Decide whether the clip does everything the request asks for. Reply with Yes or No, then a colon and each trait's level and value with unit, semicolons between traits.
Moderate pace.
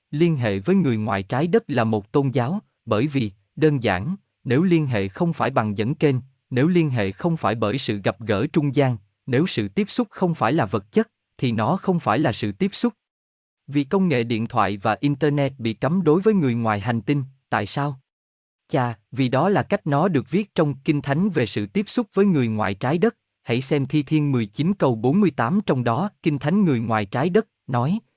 Yes: average, 220 wpm